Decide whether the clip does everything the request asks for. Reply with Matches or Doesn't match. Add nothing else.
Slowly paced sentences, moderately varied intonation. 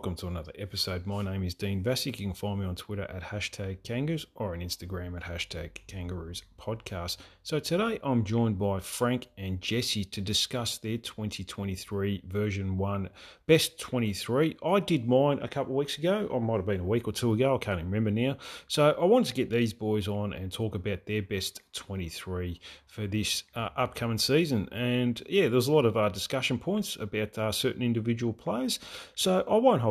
Doesn't match